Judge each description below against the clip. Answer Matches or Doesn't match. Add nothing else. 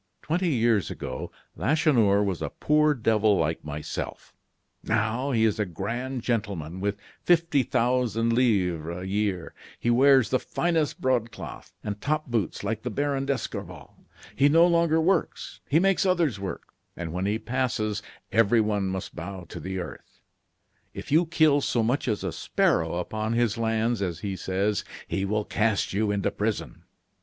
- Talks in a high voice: Doesn't match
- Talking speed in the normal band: Matches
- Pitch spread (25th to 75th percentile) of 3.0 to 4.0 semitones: Doesn't match